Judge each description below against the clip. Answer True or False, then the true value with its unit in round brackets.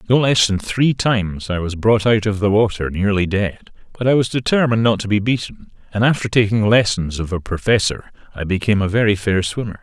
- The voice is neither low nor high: False (105 Hz)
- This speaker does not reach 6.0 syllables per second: True (5.8 syllables/s)